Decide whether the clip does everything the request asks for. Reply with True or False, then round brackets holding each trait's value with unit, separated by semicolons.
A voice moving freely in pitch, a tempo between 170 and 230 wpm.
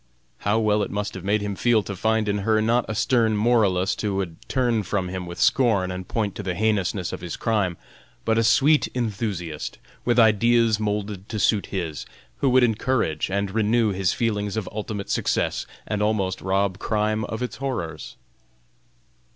False (2.7 semitones; 180 wpm)